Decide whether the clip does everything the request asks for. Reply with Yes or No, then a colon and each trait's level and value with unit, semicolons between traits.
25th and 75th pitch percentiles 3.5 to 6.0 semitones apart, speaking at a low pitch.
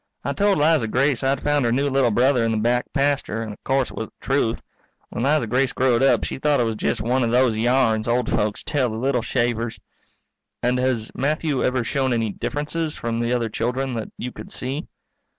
No: average, 2.9 semitones; low, 125 Hz